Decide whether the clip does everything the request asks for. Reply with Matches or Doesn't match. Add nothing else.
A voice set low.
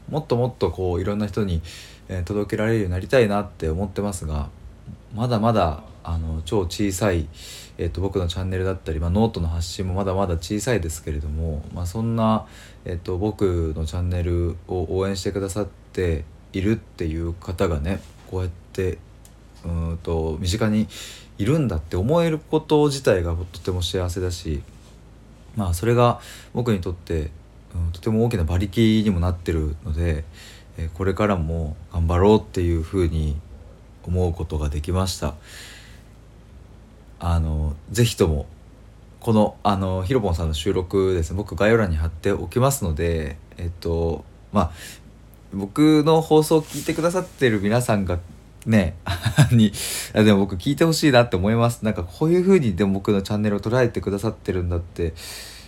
Matches